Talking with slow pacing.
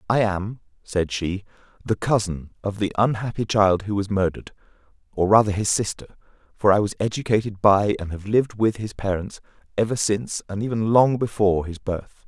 No: average, 175 wpm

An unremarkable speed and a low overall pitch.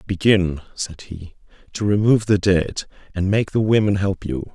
Yes: average, 170 wpm; very low, 95 Hz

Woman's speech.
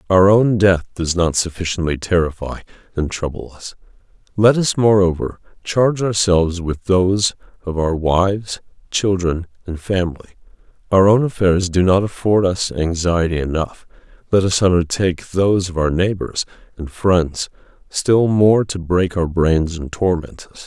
No: male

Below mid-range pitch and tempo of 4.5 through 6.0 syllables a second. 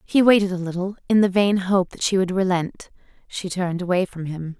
No: medium, 185 Hz; 5.5 syllables/s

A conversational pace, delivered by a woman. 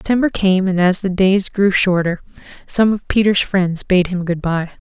Yes: average, 195 wpm; female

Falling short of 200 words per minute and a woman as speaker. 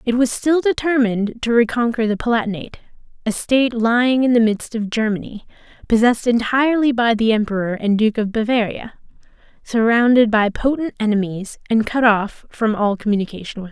Yes: average, 160 wpm; female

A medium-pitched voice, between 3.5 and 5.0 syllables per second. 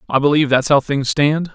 No: medium, 145 Hz; 6.0 syllables/s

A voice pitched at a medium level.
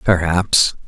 No: very low, 90 Hz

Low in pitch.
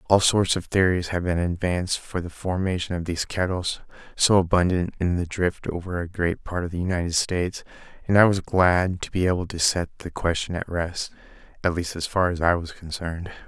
Yes: very low, 90 Hz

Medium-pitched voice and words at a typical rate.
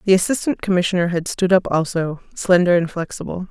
Yes: medium, 180 Hz; average, 170 wpm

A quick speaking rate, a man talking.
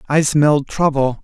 No: average, 145 wpm; male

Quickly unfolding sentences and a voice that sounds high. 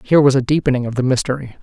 No: fast, 260 wpm; low, 135 Hz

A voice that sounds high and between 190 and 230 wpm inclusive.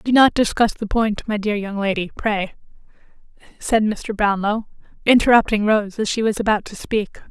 No: high, 215 Hz; average, 170 wpm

